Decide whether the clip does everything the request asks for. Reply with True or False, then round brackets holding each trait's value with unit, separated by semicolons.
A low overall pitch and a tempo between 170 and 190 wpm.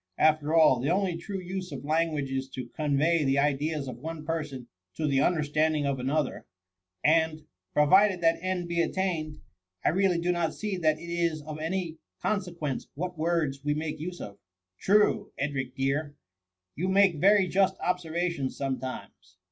False (155 Hz; 180 wpm)